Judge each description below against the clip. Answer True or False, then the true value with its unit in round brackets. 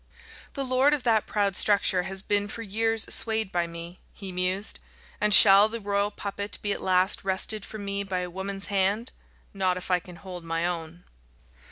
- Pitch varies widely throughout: False (2.5 semitones)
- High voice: True (195 Hz)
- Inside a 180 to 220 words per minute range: True (190 wpm)